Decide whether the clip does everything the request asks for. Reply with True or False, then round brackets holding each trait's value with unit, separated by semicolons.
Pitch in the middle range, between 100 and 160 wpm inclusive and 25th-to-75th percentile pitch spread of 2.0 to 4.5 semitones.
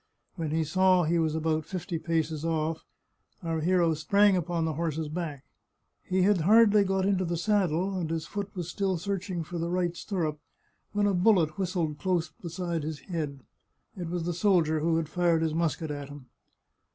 False (170 Hz; 185 wpm; 2.8 semitones)